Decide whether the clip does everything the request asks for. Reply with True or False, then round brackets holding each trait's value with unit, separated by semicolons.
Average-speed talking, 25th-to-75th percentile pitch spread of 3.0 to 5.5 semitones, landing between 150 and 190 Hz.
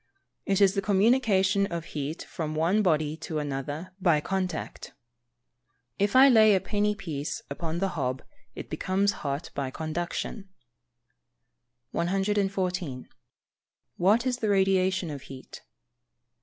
False (130 wpm; 4.3 semitones; 185 Hz)